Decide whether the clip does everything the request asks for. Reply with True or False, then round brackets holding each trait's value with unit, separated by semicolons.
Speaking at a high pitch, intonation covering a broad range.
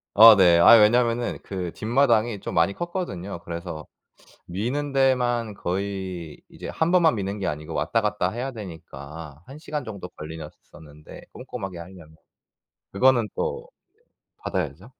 False (100 Hz; 6.2 semitones)